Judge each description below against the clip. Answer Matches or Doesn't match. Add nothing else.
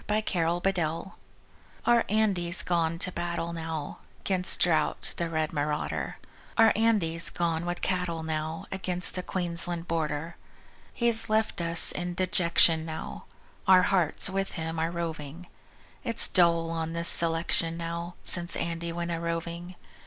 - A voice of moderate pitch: Matches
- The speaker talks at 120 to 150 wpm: Matches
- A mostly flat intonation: Matches